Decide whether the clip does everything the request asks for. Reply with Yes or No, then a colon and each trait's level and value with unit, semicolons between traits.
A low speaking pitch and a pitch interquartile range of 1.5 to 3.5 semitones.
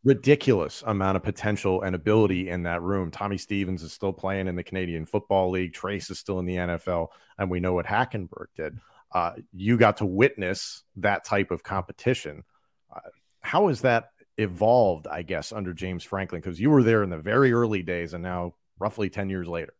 Yes: very low, 95 Hz; average, 2.8 semitones